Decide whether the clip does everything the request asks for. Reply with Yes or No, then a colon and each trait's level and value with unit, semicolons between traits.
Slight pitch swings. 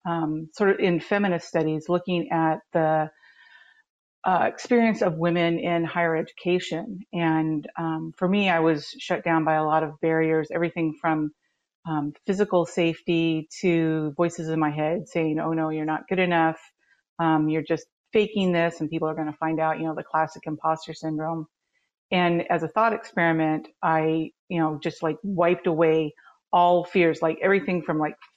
Yes: narrow, 2.0 semitones